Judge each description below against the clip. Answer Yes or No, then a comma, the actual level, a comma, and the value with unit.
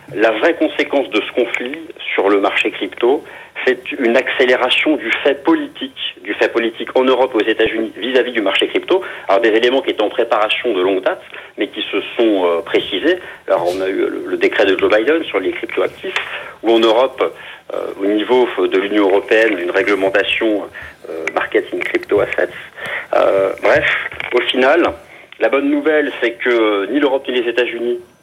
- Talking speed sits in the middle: Yes, average, 185 wpm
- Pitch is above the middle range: Yes, very high, 325 Hz